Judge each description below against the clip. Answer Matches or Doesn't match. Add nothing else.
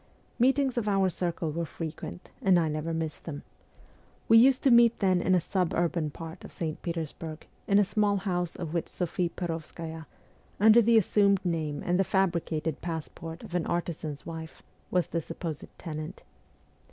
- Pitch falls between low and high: Matches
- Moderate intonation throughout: Matches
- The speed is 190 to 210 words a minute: Doesn't match